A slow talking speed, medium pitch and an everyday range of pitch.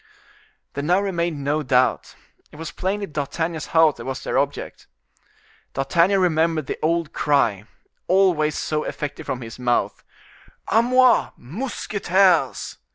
Yes: slow, 130 wpm; medium, 160 Hz; average, 4.6 semitones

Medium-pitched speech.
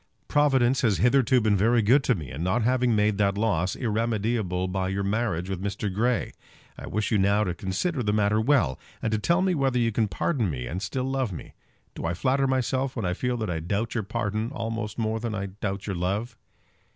No: low, 110 Hz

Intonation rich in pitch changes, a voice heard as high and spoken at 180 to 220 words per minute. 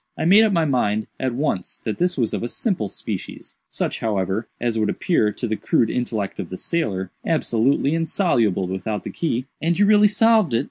No: wide, 8.0 semitones; low, 120 Hz; average, 195 wpm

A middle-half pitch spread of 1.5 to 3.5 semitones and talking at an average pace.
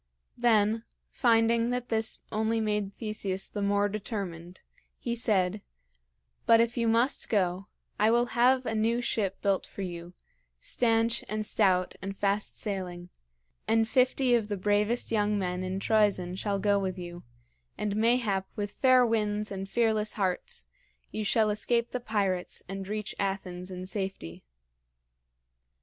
Yes: average, 2.8 semitones; average, 145 wpm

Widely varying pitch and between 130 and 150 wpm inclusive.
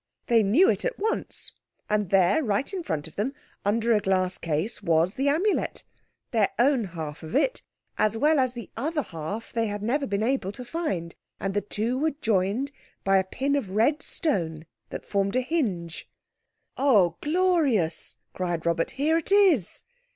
No: wide, 7.0 semitones; average, 170 wpm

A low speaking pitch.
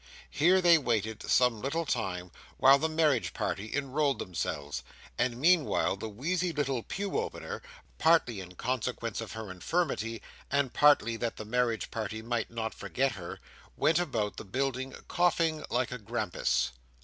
Yes: low, 125 Hz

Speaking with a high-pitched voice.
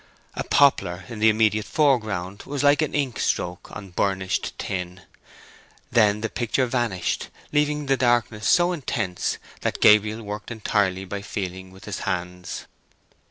No: low, 105 Hz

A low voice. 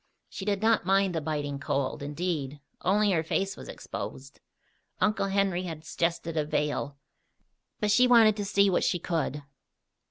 No: medium, 175 Hz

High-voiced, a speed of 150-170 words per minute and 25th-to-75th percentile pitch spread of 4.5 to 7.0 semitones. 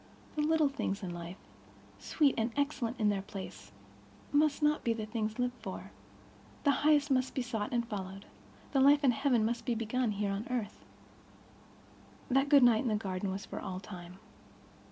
No: high, 235 Hz; average, 180 wpm; average, 5.1 semitones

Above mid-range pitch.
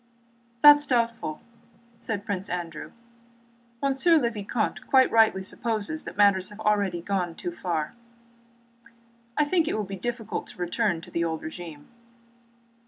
Yes: high, 205 Hz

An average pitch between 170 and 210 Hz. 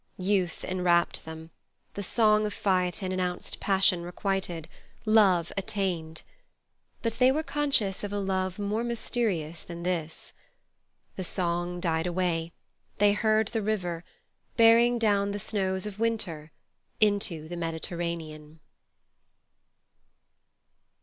Yes: high, 190 Hz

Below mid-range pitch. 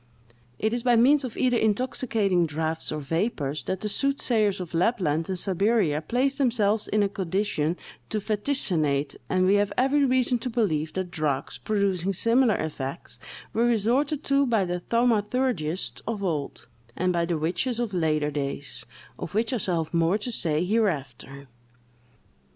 No: high, 200 Hz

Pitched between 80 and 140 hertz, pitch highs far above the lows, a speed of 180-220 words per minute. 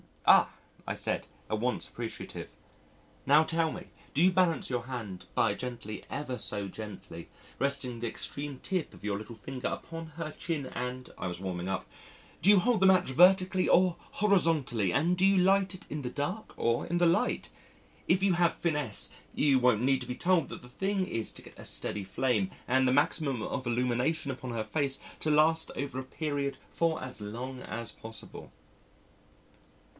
Yes: low, 135 Hz; wide, 5.9 semitones; average, 185 wpm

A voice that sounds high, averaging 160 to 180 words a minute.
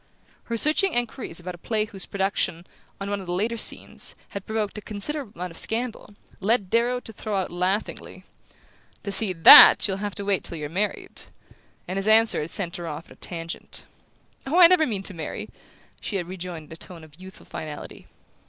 No: high, 195 Hz; average, 200 wpm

